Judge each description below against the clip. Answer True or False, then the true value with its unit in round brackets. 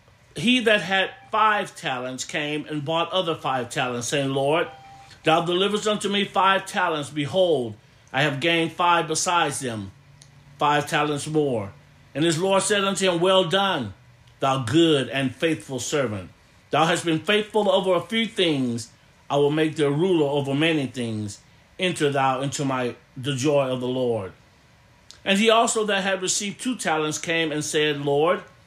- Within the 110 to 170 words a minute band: True (165 wpm)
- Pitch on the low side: False (150 Hz)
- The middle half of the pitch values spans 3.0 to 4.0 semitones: False (5.5 semitones)